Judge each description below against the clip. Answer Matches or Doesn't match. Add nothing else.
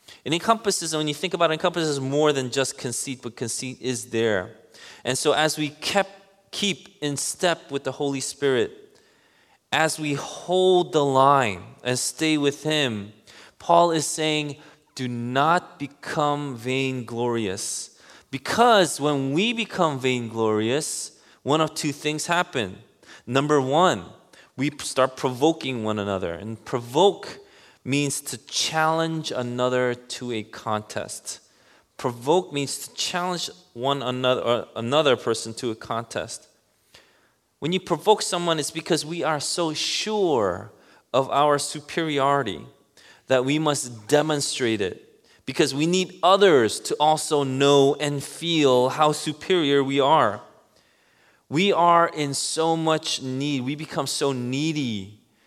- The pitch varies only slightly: Doesn't match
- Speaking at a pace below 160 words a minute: Matches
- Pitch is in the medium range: Matches